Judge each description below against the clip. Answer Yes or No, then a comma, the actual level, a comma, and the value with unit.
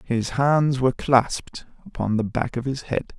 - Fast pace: No, average, 190 wpm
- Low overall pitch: Yes, low, 125 Hz